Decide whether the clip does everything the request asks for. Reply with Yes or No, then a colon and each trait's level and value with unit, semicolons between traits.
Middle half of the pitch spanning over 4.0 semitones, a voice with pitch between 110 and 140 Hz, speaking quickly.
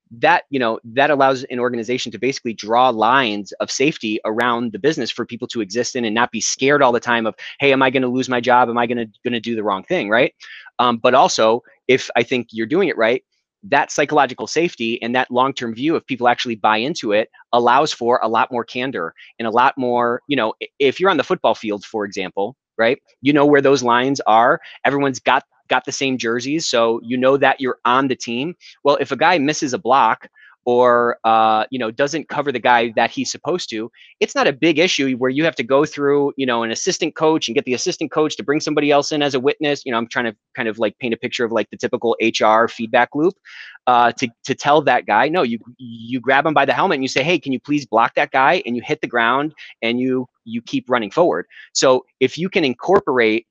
No: average, 3.2 semitones; low, 125 Hz; fast, 240 wpm